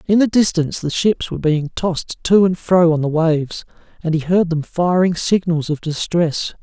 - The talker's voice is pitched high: No, medium, 170 Hz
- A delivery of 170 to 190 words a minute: No, average, 200 wpm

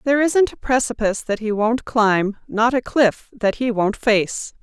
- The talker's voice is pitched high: Yes, high, 230 Hz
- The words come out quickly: No, average, 195 wpm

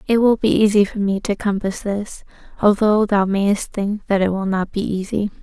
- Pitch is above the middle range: Yes, high, 205 Hz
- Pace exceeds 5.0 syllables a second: No, 4.8 syllables/s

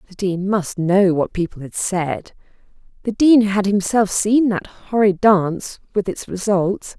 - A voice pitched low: No, high, 195 Hz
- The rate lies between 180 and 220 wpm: No, average, 165 wpm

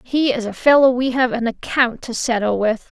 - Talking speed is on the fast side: Yes, fast, 220 wpm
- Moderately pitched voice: No, high, 240 Hz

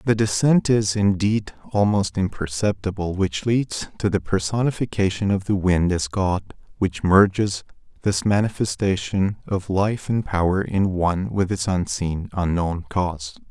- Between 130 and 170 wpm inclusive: Yes, average, 140 wpm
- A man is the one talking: Yes, male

